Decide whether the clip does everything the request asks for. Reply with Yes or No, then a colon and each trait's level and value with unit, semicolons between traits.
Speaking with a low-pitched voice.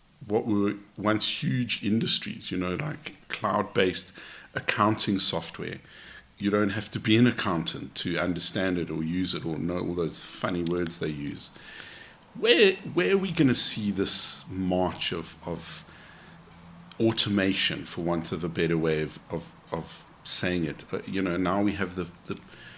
Yes: very low, 95 Hz